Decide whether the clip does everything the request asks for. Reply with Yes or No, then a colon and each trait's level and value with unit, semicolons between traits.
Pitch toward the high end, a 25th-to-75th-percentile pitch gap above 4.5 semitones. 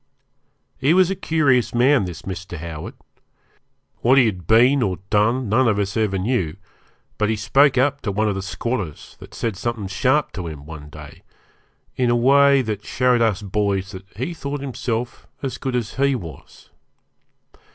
No: low, 115 Hz; average, 5.2 semitones